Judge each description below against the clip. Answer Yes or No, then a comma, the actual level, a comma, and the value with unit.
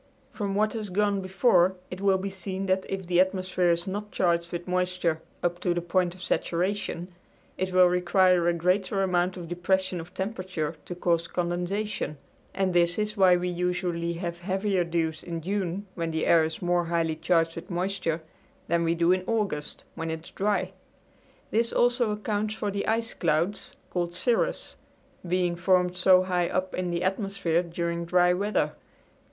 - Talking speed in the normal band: Yes, average, 175 wpm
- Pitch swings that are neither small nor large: No, narrow, 2.0 semitones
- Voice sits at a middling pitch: Yes, medium, 180 Hz